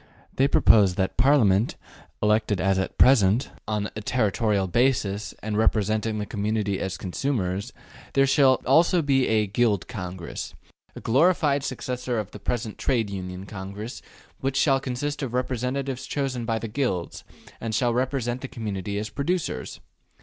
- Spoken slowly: No, average, 155 wpm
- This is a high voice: No, low, 115 Hz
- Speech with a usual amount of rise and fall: Yes, average, 4.6 semitones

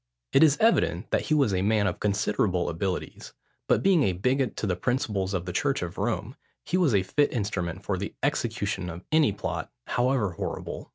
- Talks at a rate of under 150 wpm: No, average, 195 wpm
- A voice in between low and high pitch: No, low, 105 Hz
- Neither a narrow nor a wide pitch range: No, wide, 6.4 semitones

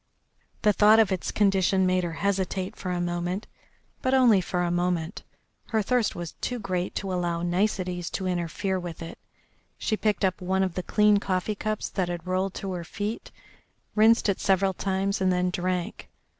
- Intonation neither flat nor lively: No, narrow, 2.3 semitones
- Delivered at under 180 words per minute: No, average, 185 wpm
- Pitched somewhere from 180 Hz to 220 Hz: Yes, medium, 185 Hz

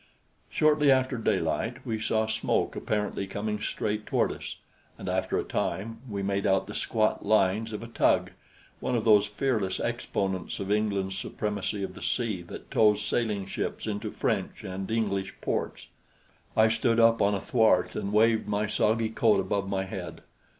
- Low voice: Yes, low, 105 Hz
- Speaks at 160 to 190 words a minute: Yes, average, 170 wpm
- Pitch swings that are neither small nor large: No, narrow, 2.2 semitones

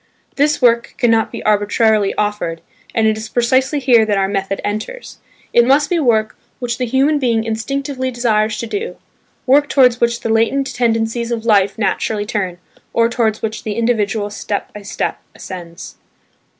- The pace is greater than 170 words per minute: No, average, 165 wpm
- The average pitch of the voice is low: No, high, 225 Hz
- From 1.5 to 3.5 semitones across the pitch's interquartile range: Yes, average, 2.9 semitones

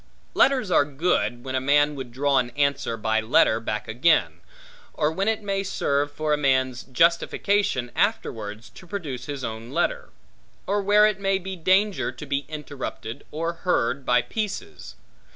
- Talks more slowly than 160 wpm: No, average, 165 wpm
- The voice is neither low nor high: Yes, medium, 145 Hz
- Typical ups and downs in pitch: No, wide, 7.3 semitones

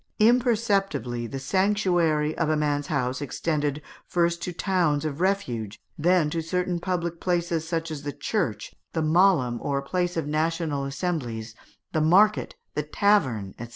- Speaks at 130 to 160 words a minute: Yes, average, 155 wpm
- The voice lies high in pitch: No, medium, 160 Hz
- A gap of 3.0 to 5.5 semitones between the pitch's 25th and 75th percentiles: Yes, average, 4.0 semitones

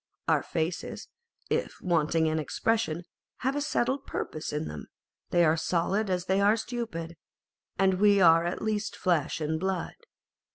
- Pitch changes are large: No, average, 4.3 semitones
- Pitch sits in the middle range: Yes, medium, 180 Hz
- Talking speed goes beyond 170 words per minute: No, average, 155 wpm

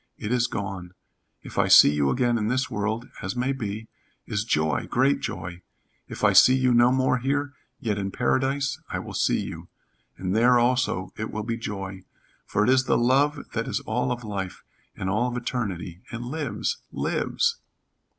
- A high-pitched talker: No, low, 120 Hz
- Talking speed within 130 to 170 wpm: No, average, 185 wpm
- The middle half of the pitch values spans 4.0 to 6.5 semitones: Yes, average, 4.3 semitones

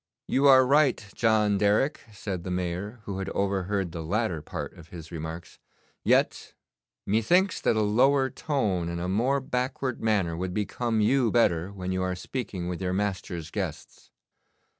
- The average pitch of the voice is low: Yes, low, 100 Hz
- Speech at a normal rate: Yes, average, 160 wpm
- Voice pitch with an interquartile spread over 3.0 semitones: Yes, average, 5.1 semitones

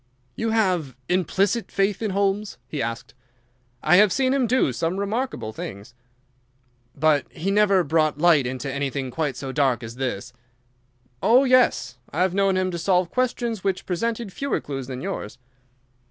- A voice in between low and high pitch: Yes, medium, 180 Hz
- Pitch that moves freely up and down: Yes, wide, 7.1 semitones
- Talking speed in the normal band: Yes, average, 155 wpm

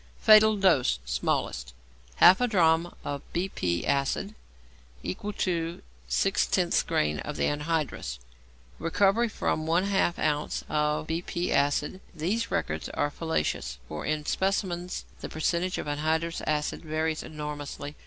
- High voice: No, medium, 160 Hz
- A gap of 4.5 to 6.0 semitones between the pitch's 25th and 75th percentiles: No, average, 3.6 semitones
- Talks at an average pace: No, slow, 130 wpm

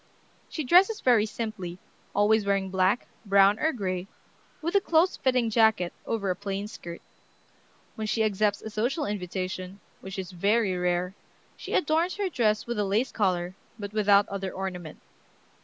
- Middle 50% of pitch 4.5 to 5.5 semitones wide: No, average, 3.5 semitones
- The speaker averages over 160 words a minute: No, average, 155 wpm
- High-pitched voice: Yes, high, 205 Hz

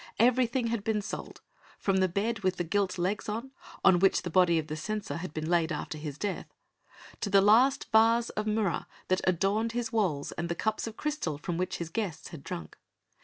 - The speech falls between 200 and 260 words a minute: Yes, fast, 205 wpm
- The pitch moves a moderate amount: Yes, average, 4.6 semitones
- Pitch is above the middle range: Yes, high, 195 Hz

